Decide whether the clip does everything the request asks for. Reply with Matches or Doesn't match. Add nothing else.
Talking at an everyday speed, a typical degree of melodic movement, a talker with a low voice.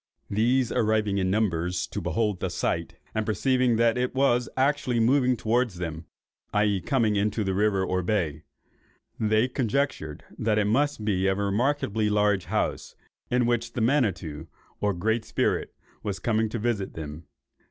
Matches